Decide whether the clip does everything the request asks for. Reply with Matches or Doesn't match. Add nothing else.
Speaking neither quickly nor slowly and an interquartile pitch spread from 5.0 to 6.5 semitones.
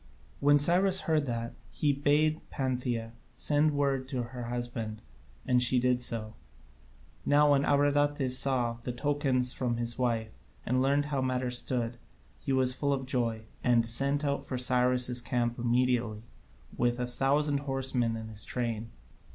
Doesn't match